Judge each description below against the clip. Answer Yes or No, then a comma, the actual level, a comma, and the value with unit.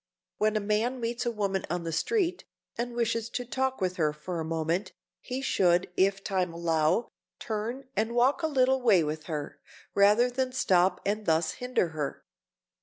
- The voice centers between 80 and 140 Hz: No, high, 210 Hz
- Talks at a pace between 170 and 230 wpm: Yes, average, 180 wpm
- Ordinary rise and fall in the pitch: No, wide, 6.2 semitones